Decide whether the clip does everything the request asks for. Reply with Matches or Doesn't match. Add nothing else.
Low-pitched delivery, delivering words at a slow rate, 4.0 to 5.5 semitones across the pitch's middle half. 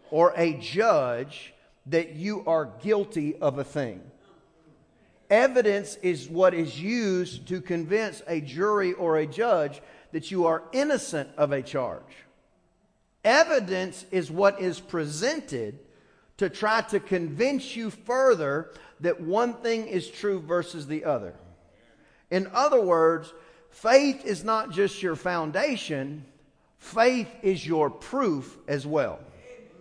Doesn't match